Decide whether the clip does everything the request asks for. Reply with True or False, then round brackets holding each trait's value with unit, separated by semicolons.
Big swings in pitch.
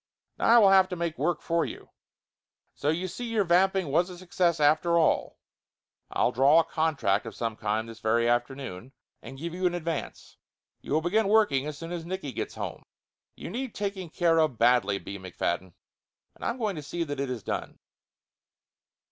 True (5.9 semitones)